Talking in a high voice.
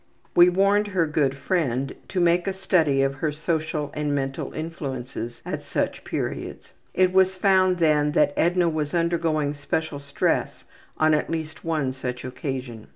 No: medium, 155 Hz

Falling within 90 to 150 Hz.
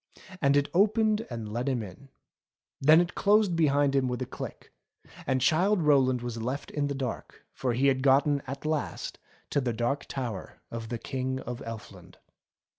Yes: low, 135 Hz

